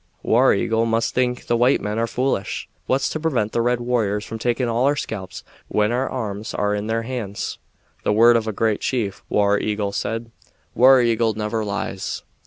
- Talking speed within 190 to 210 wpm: Yes, average, 195 wpm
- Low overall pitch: Yes, low, 115 Hz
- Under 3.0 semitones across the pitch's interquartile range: Yes, narrow, 2.6 semitones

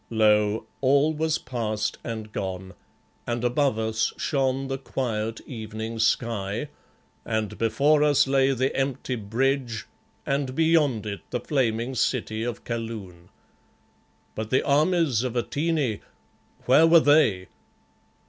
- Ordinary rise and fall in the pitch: Yes, average, 3.9 semitones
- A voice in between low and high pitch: No, low, 120 Hz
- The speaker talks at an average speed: No, slow, 120 wpm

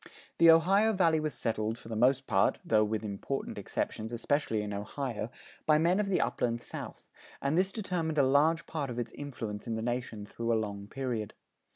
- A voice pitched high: No, low, 125 Hz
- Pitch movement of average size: No, wide, 6.2 semitones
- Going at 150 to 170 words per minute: No, average, 195 wpm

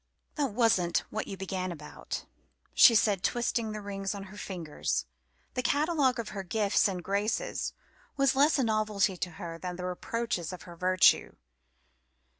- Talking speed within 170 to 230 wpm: No, average, 160 wpm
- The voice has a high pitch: Yes, high, 200 Hz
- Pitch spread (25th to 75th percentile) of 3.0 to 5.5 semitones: Yes, average, 4.1 semitones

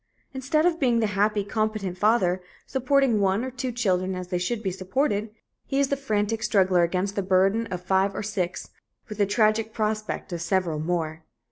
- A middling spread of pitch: Yes, average, 3.7 semitones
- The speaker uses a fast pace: No, average, 190 wpm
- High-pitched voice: Yes, high, 205 Hz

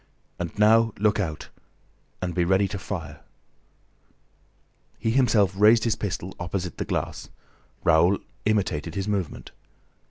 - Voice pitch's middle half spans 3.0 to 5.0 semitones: Yes, average, 3.3 semitones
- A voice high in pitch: No, low, 100 Hz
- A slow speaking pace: Yes, slow, 125 wpm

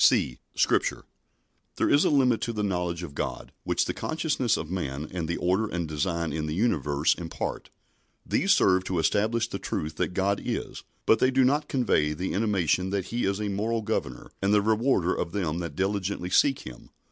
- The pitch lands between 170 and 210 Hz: No, very low, 95 Hz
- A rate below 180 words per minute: No, average, 195 wpm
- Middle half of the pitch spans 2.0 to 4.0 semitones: No, average, 4.8 semitones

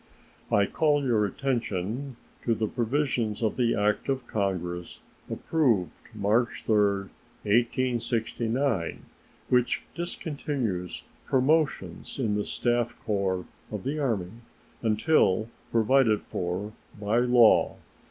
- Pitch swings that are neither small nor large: Yes, average, 4.0 semitones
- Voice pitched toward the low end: Yes, low, 115 Hz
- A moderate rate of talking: No, slow, 105 wpm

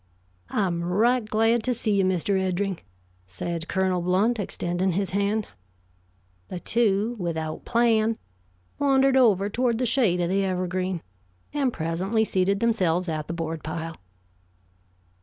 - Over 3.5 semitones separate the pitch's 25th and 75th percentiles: Yes, average, 4.2 semitones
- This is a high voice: Yes, high, 195 Hz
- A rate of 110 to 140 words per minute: Yes, slow, 135 wpm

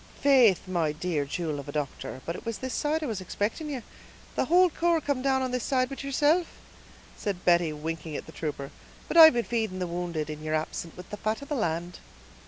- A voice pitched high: Yes, high, 195 Hz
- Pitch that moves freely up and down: Yes, wide, 8.9 semitones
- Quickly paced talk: Yes, fast, 225 wpm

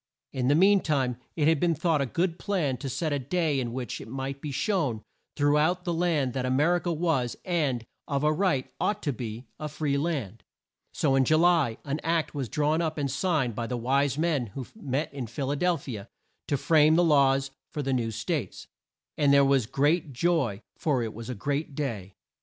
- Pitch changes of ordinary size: Yes, average, 4.0 semitones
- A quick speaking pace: Yes, fast, 220 wpm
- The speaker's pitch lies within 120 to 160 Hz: Yes, medium, 140 Hz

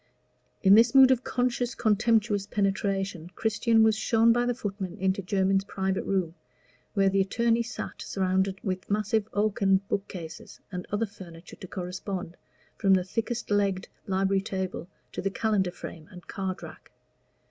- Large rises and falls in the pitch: No, narrow, 2.6 semitones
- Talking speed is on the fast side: No, average, 150 wpm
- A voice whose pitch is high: Yes, high, 195 Hz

